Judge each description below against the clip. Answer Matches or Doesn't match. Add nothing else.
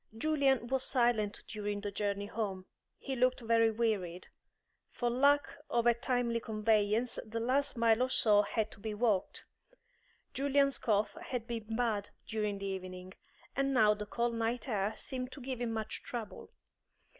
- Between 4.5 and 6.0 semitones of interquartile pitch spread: Doesn't match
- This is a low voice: Doesn't match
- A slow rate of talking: Doesn't match